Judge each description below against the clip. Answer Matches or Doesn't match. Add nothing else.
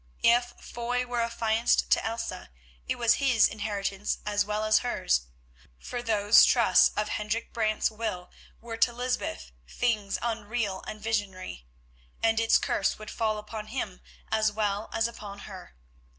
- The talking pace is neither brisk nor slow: Matches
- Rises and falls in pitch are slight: Matches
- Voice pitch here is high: Matches